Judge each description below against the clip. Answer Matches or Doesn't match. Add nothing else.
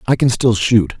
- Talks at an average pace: Doesn't match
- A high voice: Doesn't match